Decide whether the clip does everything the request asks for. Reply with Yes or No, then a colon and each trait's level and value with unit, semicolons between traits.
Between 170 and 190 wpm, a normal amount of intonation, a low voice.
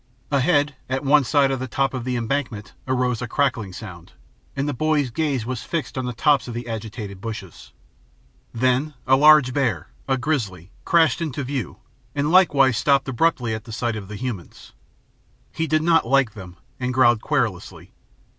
Yes: average, 175 wpm; average, 4.0 semitones; low, 130 Hz